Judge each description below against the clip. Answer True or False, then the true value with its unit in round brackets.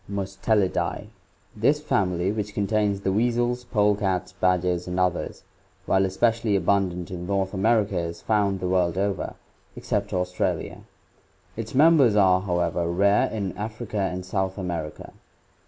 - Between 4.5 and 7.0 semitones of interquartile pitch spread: False (2.6 semitones)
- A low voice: True (95 Hz)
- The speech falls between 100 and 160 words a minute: True (135 wpm)